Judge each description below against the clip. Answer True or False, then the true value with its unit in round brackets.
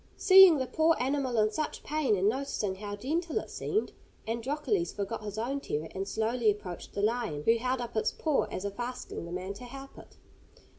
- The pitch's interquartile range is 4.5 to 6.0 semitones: True (5.4 semitones)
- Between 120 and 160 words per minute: False (200 wpm)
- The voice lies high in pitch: True (235 Hz)